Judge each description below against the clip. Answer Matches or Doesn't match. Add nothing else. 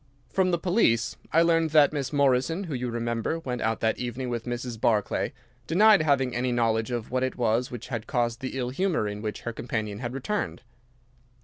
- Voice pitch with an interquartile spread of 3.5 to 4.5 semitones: Matches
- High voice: Doesn't match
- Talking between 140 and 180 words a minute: Doesn't match